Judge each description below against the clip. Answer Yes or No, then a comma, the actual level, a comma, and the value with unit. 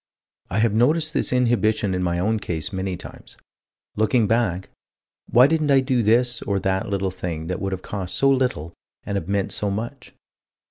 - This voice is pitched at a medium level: No, low, 105 Hz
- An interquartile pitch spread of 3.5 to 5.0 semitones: Yes, average, 4.5 semitones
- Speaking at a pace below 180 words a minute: No, average, 185 wpm